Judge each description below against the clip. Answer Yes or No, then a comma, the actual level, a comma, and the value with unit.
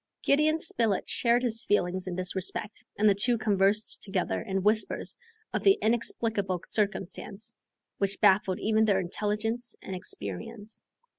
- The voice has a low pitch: No, high, 210 Hz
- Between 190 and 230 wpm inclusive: No, average, 140 wpm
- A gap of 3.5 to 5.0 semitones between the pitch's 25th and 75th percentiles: No, average, 2.8 semitones